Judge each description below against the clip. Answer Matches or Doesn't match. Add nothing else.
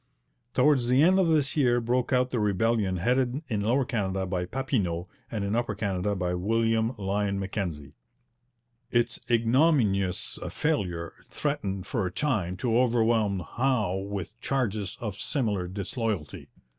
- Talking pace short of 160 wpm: Matches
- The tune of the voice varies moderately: Matches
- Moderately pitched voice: Doesn't match